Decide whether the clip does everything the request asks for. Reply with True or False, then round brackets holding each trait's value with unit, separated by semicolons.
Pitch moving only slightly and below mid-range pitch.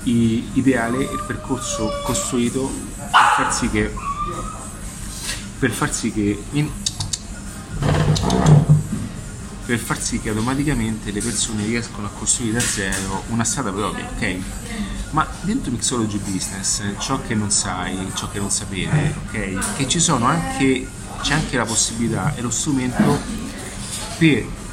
False (3.6 semitones; 110 Hz)